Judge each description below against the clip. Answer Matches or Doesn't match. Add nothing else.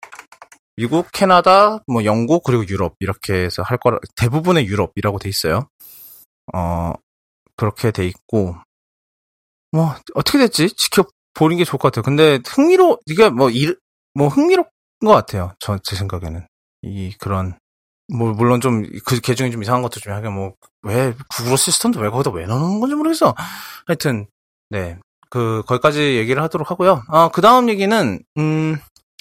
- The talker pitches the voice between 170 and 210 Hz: Doesn't match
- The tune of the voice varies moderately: Doesn't match